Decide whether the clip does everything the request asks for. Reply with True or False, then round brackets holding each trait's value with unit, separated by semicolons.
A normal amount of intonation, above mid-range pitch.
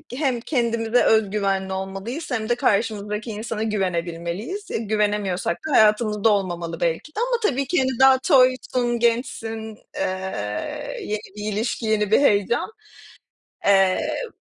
True (4.0 semitones; 215 Hz)